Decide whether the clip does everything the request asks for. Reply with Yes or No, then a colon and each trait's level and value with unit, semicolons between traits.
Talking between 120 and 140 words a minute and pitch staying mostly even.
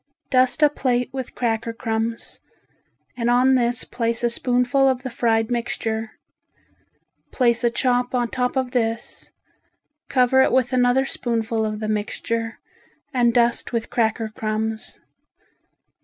Yes: slow, 135 wpm; narrow, 1.8 semitones